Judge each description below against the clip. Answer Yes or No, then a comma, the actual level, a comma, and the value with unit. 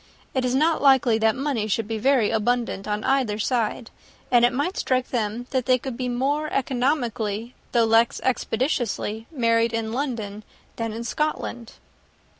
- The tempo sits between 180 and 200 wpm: No, average, 160 wpm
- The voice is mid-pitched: No, high, 240 Hz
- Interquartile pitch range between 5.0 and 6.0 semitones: No, average, 2.8 semitones